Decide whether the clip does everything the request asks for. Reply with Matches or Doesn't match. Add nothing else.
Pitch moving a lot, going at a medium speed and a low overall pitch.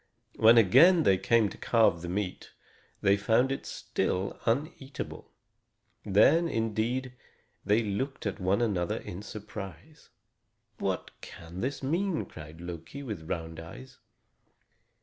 Doesn't match